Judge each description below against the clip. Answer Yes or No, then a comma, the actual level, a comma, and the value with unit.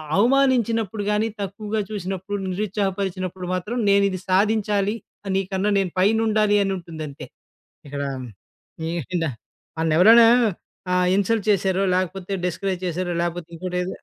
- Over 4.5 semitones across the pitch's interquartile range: No, narrow, 2.6 semitones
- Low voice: No, high, 195 Hz